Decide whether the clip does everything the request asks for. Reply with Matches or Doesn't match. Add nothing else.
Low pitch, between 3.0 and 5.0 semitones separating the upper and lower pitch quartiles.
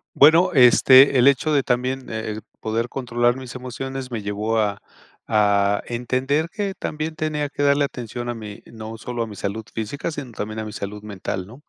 Matches